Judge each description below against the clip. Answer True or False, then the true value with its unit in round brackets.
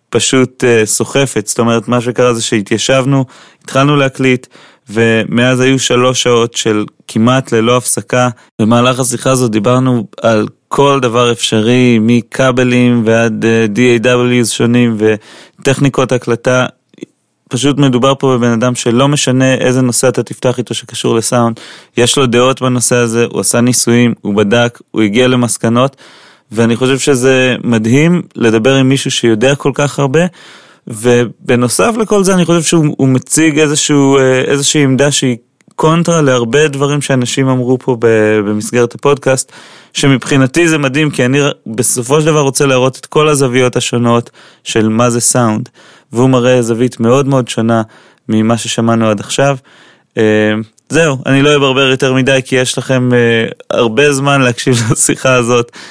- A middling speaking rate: True (140 wpm)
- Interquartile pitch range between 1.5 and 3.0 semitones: True (2.4 semitones)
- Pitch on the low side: True (125 Hz)